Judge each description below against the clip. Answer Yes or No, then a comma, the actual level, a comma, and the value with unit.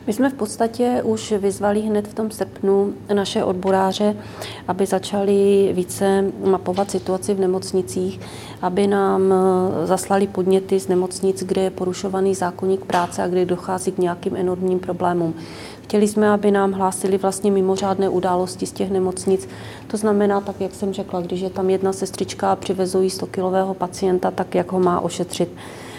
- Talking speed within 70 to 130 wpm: No, average, 155 wpm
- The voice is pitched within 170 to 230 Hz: Yes, high, 190 Hz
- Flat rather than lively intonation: Yes, narrow, 1.3 semitones